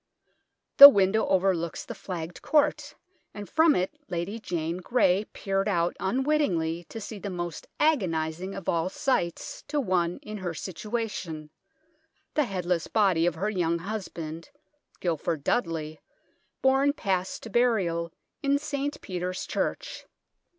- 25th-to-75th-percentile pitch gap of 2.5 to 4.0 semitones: No, average, 5.0 semitones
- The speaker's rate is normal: No, slow, 130 wpm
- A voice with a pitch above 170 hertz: Yes, high, 190 Hz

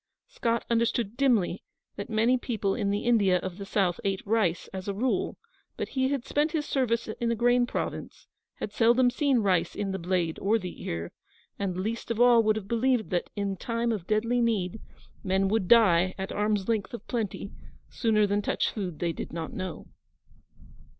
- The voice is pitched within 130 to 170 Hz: No, high, 215 Hz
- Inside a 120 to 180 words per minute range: No, average, 190 wpm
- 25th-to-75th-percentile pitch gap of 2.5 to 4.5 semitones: Yes, average, 3.5 semitones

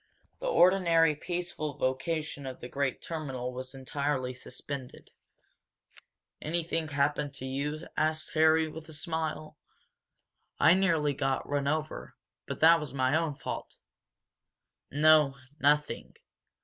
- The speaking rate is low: Yes, slow, 120 wpm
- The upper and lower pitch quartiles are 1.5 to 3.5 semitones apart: Yes, average, 2.7 semitones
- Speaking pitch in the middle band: Yes, medium, 150 Hz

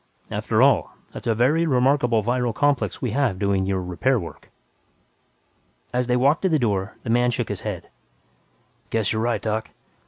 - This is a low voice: Yes, low, 120 Hz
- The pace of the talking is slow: No, average, 175 wpm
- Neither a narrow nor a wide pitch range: Yes, average, 3.5 semitones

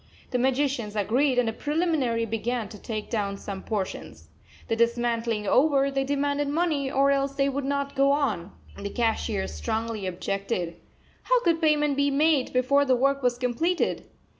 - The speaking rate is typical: Yes, average, 165 wpm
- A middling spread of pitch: Yes, average, 4.0 semitones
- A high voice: Yes, very high, 255 Hz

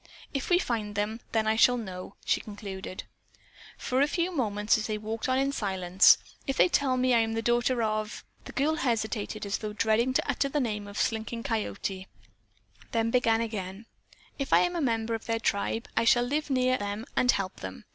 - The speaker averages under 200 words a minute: No, fast, 205 wpm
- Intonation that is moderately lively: Yes, average, 3.3 semitones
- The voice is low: No, high, 225 Hz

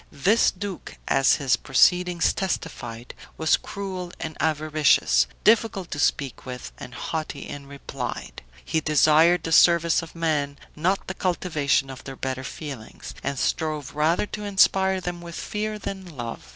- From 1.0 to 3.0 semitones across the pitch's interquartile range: No, average, 4.4 semitones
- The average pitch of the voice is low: No, medium, 160 Hz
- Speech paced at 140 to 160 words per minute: Yes, average, 150 wpm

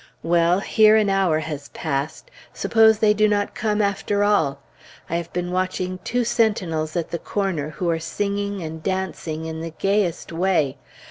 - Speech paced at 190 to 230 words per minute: No, average, 170 wpm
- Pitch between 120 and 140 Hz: No, medium, 185 Hz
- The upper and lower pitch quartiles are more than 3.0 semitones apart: Yes, average, 4.1 semitones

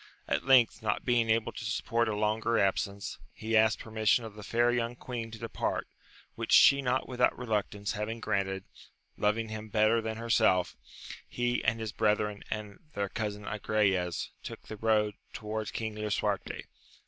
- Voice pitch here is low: Yes, low, 110 Hz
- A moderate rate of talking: Yes, average, 160 wpm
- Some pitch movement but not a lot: No, narrow, 1.5 semitones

